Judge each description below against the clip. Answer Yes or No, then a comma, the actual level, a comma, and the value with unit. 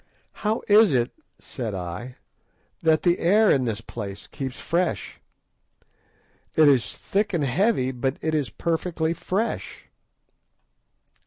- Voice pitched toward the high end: No, medium, 155 Hz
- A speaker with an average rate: No, slow, 125 wpm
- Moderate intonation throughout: No, wide, 6.4 semitones